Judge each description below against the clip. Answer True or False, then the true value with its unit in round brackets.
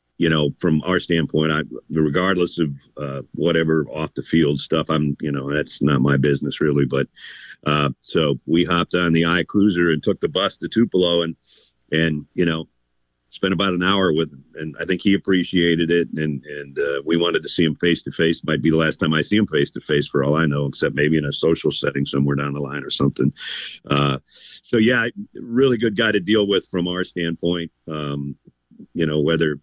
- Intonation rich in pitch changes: False (3.4 semitones)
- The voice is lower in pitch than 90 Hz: True (80 Hz)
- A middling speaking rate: False (215 wpm)